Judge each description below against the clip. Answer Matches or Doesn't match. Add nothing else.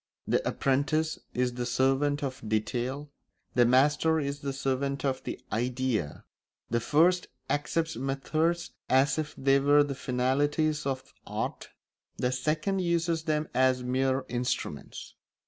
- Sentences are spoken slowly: Matches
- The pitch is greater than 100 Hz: Matches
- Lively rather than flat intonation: Doesn't match